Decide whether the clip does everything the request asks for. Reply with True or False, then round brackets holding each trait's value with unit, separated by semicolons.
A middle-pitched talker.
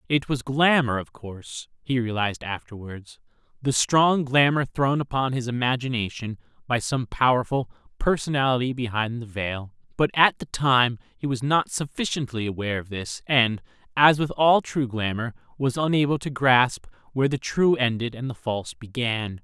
False (125 Hz)